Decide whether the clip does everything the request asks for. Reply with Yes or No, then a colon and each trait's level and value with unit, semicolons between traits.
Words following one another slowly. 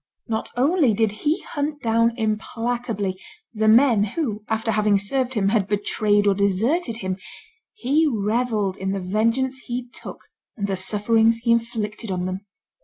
No: average, 155 wpm